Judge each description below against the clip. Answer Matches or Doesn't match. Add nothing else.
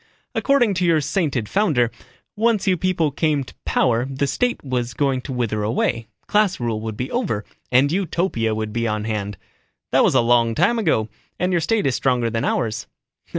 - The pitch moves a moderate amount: Doesn't match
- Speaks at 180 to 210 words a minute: Matches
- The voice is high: Doesn't match